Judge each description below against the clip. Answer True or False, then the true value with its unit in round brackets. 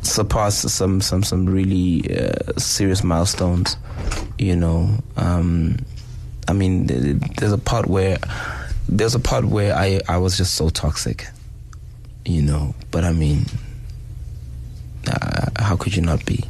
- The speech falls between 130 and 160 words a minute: True (145 wpm)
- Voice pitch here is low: True (95 Hz)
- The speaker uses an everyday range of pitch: True (4.2 semitones)